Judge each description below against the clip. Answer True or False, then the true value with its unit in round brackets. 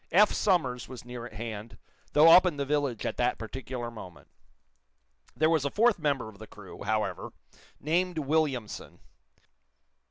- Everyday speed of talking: True (155 wpm)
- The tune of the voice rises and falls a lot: True (5.9 semitones)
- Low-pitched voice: True (130 Hz)